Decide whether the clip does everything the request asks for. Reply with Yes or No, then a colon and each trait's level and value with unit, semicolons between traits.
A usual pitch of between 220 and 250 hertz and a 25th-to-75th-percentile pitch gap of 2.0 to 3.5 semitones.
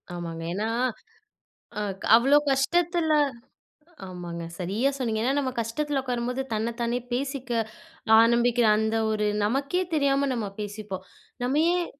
No: high, 240 Hz; average, 4.3 semitones